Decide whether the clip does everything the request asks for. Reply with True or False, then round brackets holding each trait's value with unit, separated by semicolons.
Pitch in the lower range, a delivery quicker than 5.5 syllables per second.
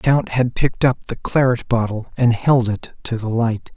False (120 Hz; 4.7 syllables/s)